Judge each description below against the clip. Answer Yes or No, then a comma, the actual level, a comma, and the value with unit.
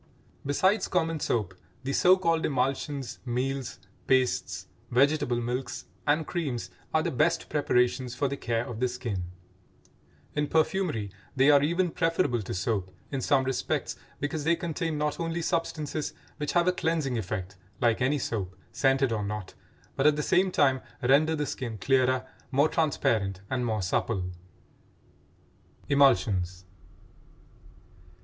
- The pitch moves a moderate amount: Yes, average, 4.5 semitones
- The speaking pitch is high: No, low, 135 Hz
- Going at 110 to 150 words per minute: Yes, average, 140 wpm